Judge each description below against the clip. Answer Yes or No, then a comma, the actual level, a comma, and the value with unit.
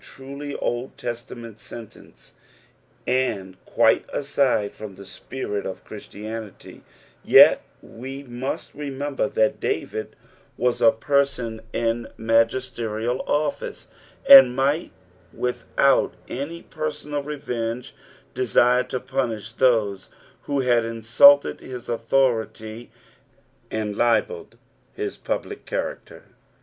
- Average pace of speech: No, slow, 100 wpm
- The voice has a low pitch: Yes, low, 125 Hz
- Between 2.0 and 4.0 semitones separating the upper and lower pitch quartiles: Yes, average, 3.4 semitones